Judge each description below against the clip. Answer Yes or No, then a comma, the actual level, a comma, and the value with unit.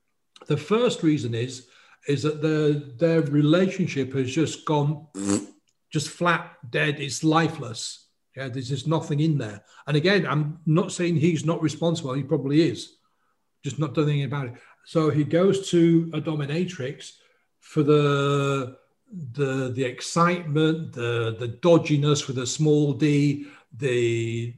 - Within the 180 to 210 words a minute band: No, average, 145 wpm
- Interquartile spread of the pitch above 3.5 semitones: No, average, 3.2 semitones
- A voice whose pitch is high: No, medium, 150 Hz